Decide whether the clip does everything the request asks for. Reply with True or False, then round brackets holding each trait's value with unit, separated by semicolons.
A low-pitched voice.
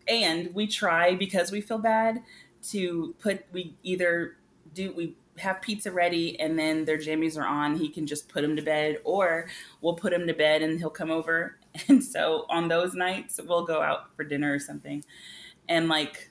False (170 Hz)